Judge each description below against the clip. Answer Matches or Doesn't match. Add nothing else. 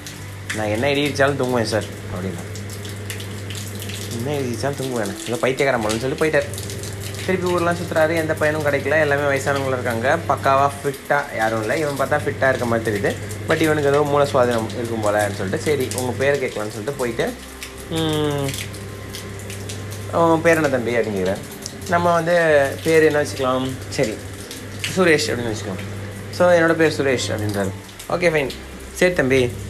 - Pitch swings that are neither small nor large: Doesn't match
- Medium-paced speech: Doesn't match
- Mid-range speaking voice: Doesn't match